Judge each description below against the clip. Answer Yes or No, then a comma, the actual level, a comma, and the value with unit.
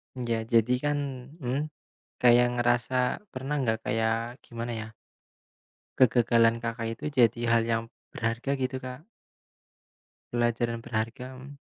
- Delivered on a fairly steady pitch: Yes, narrow, 1.8 semitones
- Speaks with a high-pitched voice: No, low, 120 Hz